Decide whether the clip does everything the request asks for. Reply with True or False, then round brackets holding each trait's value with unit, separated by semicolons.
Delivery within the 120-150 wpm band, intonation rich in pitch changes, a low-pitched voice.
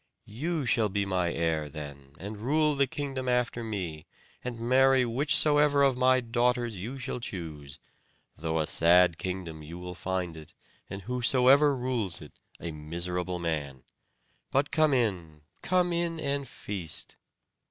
True (145 wpm; 7.7 semitones; 110 Hz)